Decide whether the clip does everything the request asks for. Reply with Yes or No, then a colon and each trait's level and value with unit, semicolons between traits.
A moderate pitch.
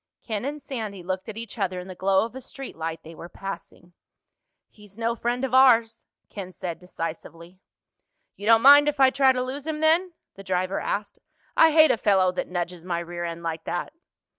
No: high, 200 Hz